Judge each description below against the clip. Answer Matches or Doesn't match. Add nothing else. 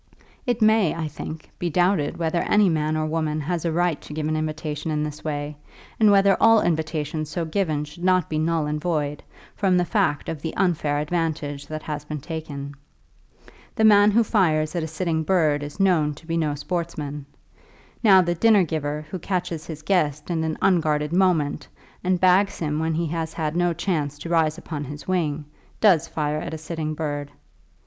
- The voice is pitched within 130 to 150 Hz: Doesn't match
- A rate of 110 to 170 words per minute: Doesn't match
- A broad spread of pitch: Doesn't match